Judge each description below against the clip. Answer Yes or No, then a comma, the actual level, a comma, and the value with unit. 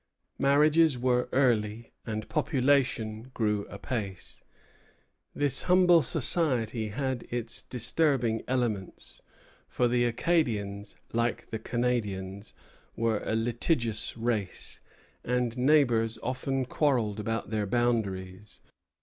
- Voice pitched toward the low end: Yes, low, 120 Hz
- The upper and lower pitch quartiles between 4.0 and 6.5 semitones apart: No, average, 3.4 semitones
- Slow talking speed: Yes, slow, 100 wpm